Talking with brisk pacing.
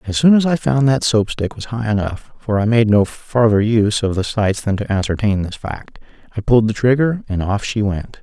Yes: fast, 235 wpm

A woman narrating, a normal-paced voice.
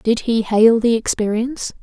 Yes: female; average, 165 wpm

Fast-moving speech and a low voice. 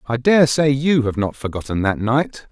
Yes: fast, 215 wpm; low, 125 Hz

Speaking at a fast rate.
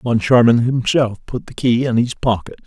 No: average, 180 wpm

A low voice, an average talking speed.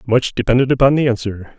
Yes: low, 120 Hz; average, 190 wpm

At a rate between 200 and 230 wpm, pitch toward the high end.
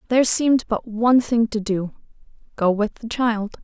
No: average, 180 wpm; high, 225 Hz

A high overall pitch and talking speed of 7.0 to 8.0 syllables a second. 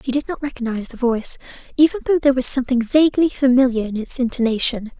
Yes: very high, 255 Hz; 7.1 syllables/s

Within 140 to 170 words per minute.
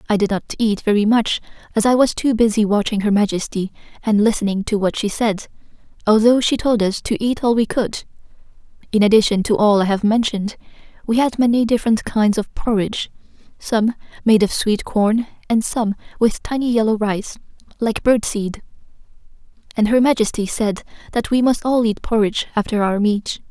No: average, 180 wpm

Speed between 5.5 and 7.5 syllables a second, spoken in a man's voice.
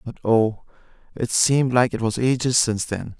No: 5.2 syllables/s; male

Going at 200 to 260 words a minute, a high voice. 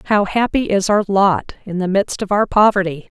Yes: fast, 205 wpm; high, 200 Hz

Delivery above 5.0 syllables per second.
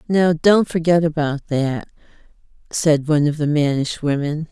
No: 4.5 syllables/s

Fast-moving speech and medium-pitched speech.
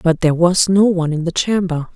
Yes: fast, 245 wpm; medium, 175 Hz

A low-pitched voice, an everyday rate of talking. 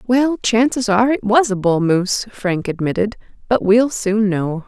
No: high, 215 Hz; average, 180 wpm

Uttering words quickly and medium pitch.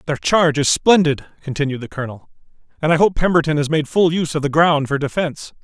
Yes: fast, 215 wpm; medium, 155 Hz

